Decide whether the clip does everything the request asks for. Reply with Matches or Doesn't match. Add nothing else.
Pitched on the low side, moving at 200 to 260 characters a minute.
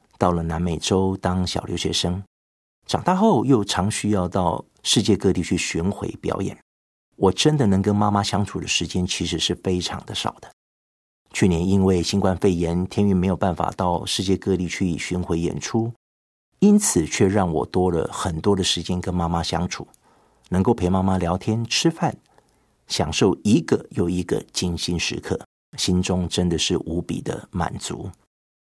Matches